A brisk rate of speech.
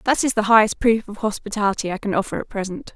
Yes: fast, 245 wpm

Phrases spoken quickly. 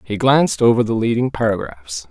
No: average, 170 wpm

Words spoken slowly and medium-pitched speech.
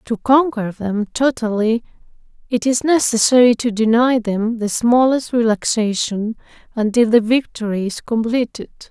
No: slow, 120 wpm; high, 230 Hz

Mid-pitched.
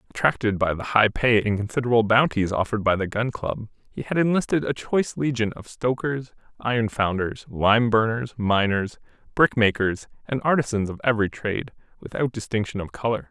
No: low, 115 Hz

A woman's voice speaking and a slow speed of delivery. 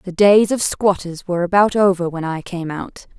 No: female; fast, 205 wpm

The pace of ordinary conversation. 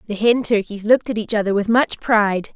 No: fast, 235 wpm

